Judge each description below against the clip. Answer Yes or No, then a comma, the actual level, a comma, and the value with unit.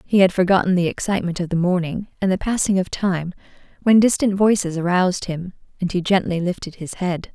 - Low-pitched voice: No, medium, 185 Hz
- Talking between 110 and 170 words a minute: No, average, 195 wpm